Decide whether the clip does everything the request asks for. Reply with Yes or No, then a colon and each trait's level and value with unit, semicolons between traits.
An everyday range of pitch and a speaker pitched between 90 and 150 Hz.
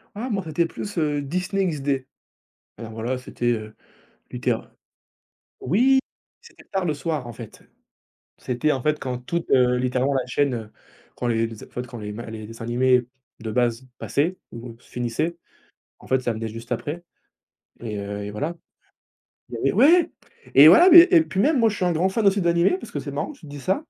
No: wide, 6.9 semitones; low, 135 Hz